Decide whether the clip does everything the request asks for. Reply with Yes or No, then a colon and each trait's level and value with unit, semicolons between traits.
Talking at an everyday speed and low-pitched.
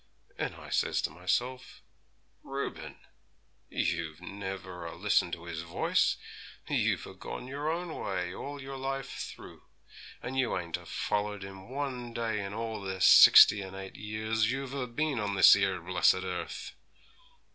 Yes: average, 155 wpm; low, 105 Hz